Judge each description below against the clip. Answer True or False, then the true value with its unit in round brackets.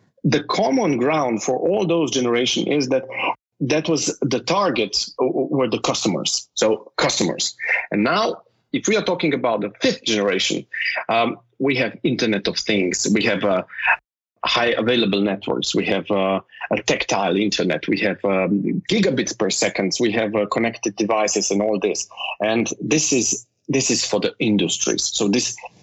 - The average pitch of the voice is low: True (110 Hz)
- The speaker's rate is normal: True (165 wpm)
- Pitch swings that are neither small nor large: True (4.9 semitones)